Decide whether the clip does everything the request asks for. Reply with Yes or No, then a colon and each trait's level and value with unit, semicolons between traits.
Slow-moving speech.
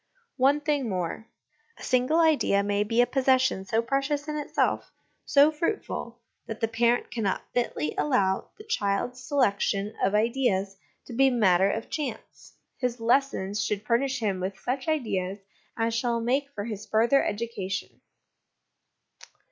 No: average, 150 wpm